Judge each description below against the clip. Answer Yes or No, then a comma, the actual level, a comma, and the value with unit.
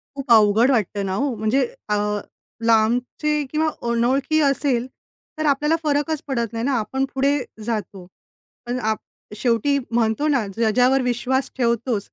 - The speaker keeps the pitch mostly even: No, average, 3.7 semitones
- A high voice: Yes, high, 245 Hz